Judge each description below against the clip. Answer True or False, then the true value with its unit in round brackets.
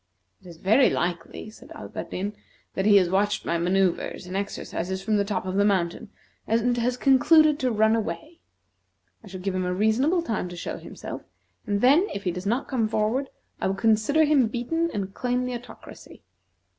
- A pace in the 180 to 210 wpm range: True (190 wpm)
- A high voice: True (215 Hz)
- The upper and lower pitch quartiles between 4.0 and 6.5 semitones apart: True (4.7 semitones)